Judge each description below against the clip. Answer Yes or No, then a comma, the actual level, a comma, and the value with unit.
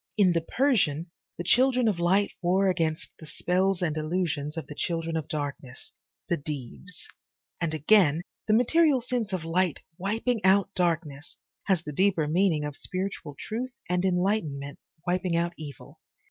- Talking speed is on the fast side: No, average, 155 wpm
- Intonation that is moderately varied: Yes, average, 4.1 semitones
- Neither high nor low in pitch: Yes, medium, 175 Hz